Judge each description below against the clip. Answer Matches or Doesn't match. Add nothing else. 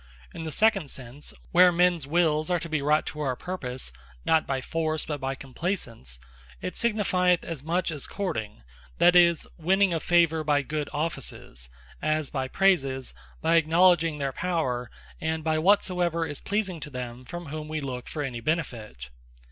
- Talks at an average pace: Matches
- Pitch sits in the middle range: Matches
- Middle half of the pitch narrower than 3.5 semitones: Doesn't match